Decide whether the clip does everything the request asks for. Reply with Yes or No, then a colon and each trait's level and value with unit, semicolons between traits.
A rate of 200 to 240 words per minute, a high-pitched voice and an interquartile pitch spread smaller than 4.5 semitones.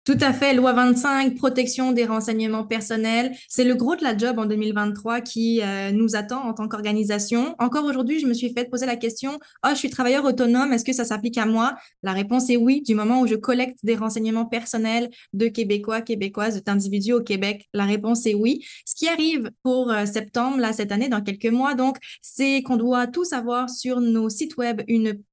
Yes: average, 210 wpm; high, 235 Hz; narrow, 2.6 semitones